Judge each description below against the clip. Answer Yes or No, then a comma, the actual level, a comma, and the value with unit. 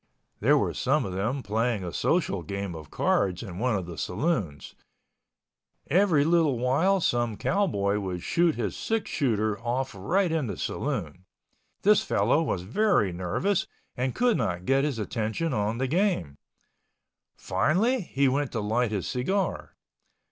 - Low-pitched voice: Yes, low, 120 Hz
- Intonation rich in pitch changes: Yes, wide, 8.7 semitones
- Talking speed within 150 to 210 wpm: Yes, average, 155 wpm